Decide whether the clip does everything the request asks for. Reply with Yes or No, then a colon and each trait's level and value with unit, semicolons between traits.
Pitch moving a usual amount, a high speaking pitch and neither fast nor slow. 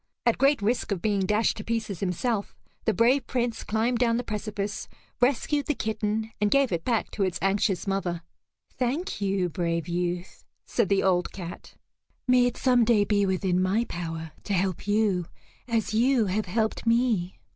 Yes: average, 3.9 semitones; high, 210 Hz; average, 175 wpm